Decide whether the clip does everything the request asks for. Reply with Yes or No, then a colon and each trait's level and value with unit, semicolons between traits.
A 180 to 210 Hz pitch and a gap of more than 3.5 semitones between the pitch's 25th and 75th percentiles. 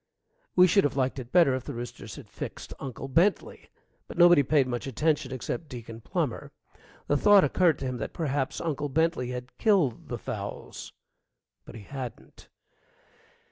No: medium, 140 Hz; average, 4.5 semitones